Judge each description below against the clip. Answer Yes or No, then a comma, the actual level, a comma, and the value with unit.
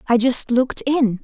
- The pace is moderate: Yes, average, 195 wpm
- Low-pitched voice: No, very high, 250 Hz